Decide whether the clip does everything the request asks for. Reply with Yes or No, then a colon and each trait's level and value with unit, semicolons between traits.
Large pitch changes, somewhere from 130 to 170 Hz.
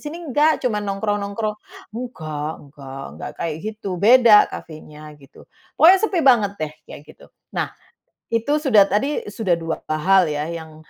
No: wide, 7.5 semitones; high, 205 Hz